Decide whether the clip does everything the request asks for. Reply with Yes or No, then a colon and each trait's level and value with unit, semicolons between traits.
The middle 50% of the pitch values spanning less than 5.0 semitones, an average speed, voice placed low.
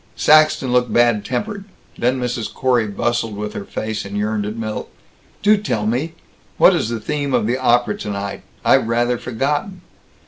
Yes: average, 3.5 semitones; average, 170 wpm; low, 120 Hz